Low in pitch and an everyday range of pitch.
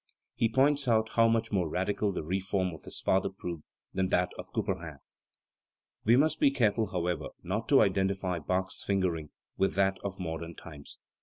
Yes: very low, 95 Hz; average, 3.7 semitones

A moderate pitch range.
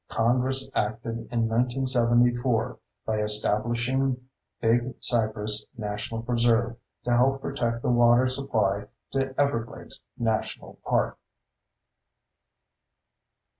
No: narrow, 2.0 semitones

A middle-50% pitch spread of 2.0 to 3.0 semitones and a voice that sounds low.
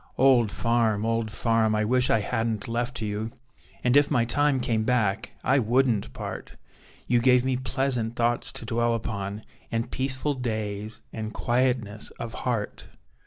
Yes: narrow, 2.4 semitones; low, 115 Hz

